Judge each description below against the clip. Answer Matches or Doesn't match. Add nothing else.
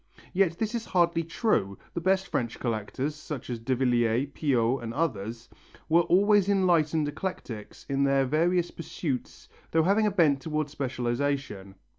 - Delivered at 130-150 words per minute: Matches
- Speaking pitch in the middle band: Matches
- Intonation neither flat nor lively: Doesn't match